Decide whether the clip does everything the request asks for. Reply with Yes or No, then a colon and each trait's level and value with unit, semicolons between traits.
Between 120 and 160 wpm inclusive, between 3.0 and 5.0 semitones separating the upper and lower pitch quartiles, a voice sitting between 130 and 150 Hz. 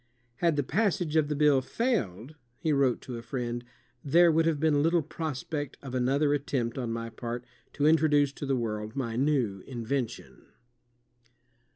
No: average, 170 wpm; average, 4.2 semitones; medium, 140 Hz